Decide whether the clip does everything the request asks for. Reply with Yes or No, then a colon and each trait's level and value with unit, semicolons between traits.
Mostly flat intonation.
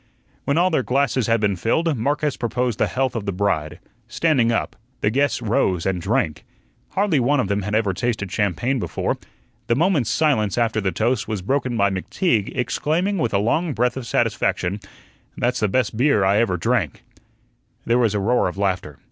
No: average, 4.9 semitones